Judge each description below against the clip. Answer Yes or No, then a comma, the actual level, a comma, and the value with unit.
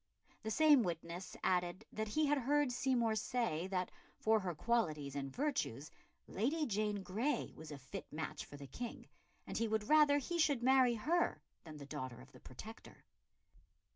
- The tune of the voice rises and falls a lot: Yes, wide, 8.4 semitones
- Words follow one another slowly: No, average, 170 wpm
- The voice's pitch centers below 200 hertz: No, high, 220 Hz